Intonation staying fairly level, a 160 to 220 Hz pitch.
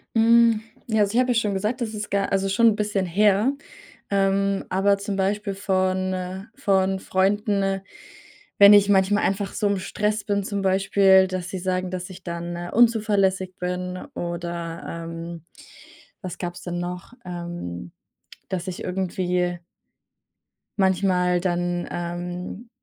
Yes: narrow, 2.3 semitones; high, 190 Hz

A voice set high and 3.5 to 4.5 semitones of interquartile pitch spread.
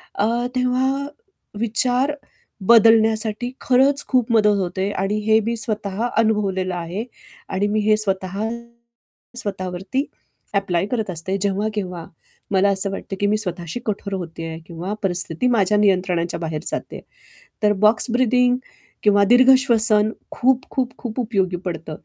Yes: high, 210 Hz; average, 3.9 semitones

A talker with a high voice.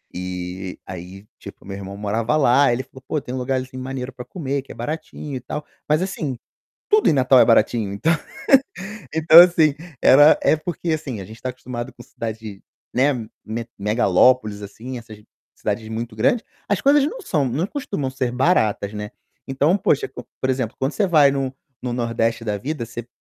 No: low, 125 Hz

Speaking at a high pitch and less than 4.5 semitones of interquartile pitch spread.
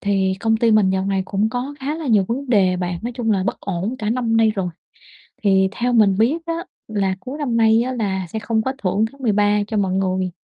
Yes: high, 215 Hz; average, 3.8 semitones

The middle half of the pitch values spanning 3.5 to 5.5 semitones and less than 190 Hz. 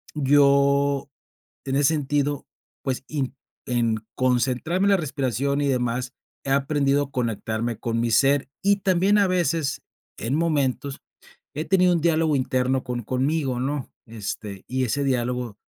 No: average, 2.9 semitones; low, 135 Hz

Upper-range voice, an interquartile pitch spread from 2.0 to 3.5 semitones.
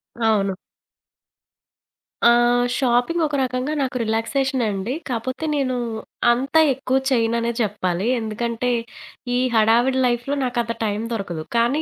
Yes: high, 240 Hz; narrow, 2.6 semitones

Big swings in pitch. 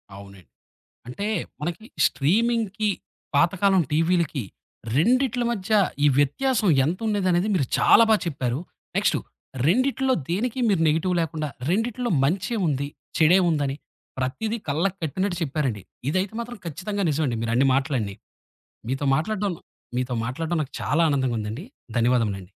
Yes: wide, 7.2 semitones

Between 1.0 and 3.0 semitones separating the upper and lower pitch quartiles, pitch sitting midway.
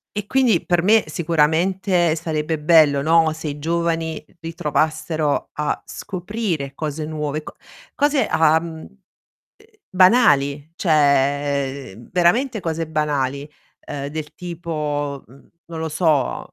Yes: average, 2.7 semitones; medium, 160 Hz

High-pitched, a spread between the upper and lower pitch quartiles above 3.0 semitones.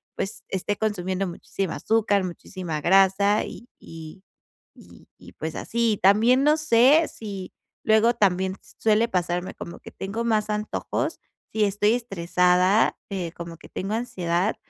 Yes: high, 195 Hz; average, 3.4 semitones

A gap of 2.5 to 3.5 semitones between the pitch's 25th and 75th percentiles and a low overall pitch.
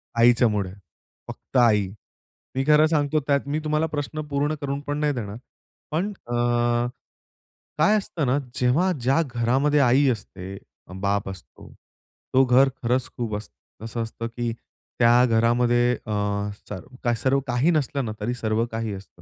No: average, 4.1 semitones; low, 125 Hz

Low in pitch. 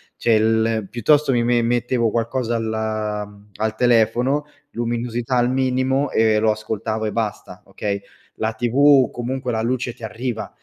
Yes: low, 115 Hz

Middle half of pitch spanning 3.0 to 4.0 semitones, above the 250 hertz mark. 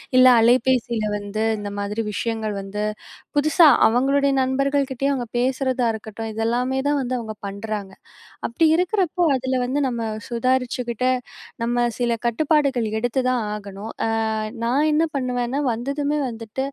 No: average, 3.3 semitones; high, 245 Hz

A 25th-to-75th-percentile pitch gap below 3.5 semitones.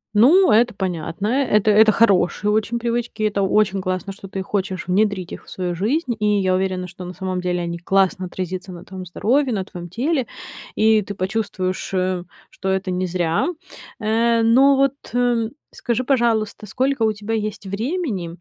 No: average, 3.8 semitones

